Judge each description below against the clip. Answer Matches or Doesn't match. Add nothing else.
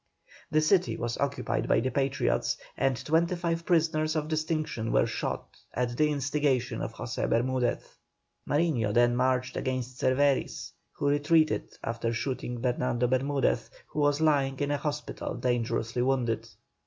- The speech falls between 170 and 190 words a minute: Doesn't match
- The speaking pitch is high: Doesn't match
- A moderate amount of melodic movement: Matches